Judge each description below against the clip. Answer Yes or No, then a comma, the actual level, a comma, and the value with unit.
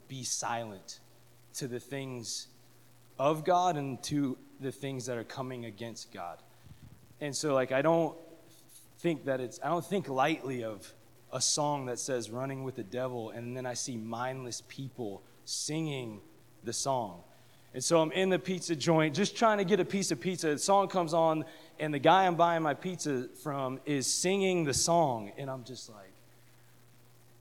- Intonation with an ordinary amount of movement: Yes, average, 5.0 semitones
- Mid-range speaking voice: No, low, 130 Hz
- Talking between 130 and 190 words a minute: Yes, average, 175 wpm